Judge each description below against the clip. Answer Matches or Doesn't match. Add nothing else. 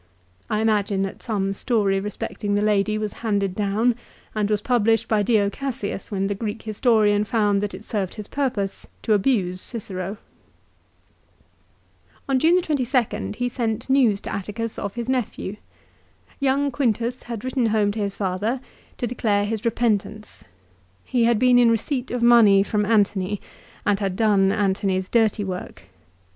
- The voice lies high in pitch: Matches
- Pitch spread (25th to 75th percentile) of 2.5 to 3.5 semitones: Matches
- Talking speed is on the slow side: Doesn't match